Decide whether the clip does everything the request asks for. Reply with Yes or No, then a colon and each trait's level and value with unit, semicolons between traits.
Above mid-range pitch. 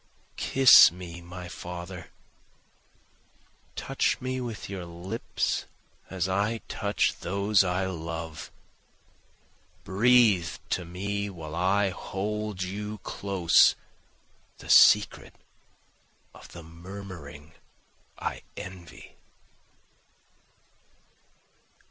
No: very low, 95 Hz